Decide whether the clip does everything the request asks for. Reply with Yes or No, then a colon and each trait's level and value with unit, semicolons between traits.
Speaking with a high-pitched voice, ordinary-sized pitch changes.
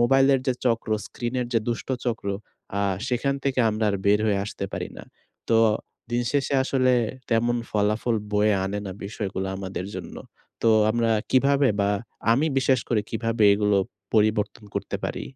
No: low, 115 Hz; average, 3.4 semitones